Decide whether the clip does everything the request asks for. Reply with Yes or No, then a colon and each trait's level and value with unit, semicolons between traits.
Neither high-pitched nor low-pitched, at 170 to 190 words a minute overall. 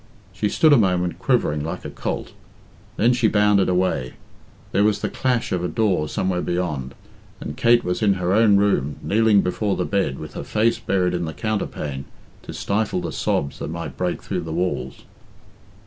No: very low, 95 Hz; average, 185 wpm